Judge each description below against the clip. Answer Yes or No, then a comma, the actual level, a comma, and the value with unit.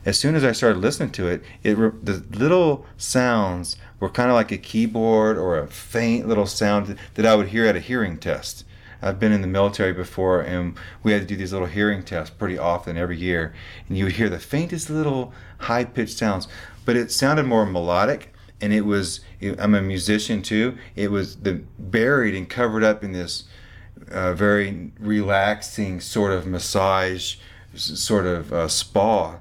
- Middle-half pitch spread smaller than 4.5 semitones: Yes, average, 2.9 semitones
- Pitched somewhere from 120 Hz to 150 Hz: No, low, 100 Hz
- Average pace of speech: Yes, average, 185 wpm